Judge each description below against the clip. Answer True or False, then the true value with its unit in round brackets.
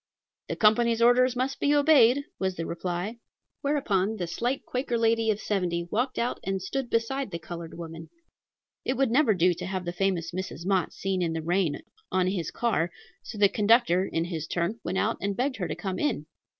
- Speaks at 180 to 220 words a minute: True (200 wpm)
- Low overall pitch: False (195 Hz)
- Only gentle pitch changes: False (5.4 semitones)